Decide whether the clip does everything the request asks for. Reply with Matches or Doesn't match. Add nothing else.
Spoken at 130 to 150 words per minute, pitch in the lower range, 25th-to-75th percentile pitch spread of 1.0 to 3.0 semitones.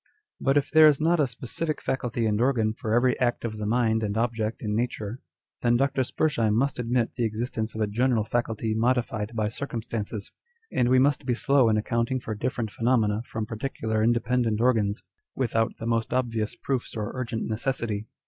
Doesn't match